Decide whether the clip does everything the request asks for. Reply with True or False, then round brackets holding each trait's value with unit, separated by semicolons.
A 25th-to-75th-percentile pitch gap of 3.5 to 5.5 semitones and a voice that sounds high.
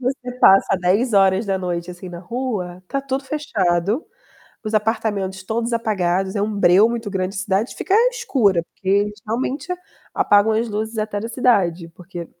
True (3.8 semitones; 205 Hz)